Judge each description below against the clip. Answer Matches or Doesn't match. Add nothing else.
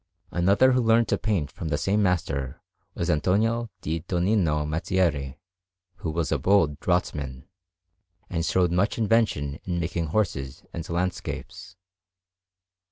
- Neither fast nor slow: Doesn't match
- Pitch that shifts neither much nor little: Matches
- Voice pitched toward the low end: Matches